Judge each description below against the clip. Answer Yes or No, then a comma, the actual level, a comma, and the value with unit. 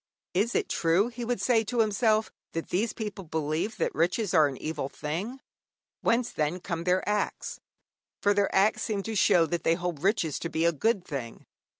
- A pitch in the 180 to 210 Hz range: Yes, medium, 185 Hz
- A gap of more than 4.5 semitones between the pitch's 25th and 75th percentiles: Yes, average, 4.9 semitones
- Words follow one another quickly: No, average, 195 wpm